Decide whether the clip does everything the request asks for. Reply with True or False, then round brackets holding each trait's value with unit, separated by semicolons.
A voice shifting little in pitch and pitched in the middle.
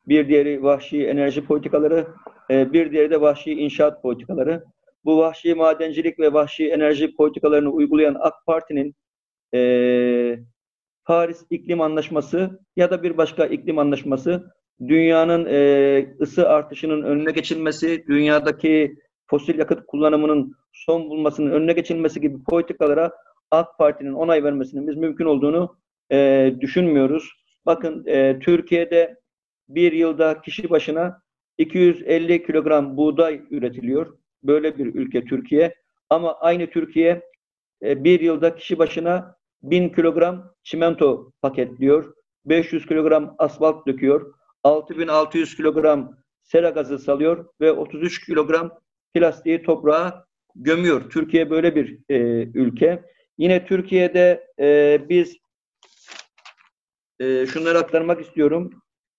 True (2.3 semitones; 155 Hz)